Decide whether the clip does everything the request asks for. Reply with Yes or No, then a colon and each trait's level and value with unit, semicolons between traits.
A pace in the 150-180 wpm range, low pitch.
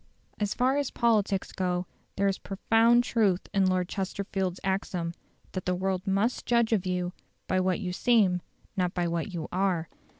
No: average, 170 wpm; high, 190 Hz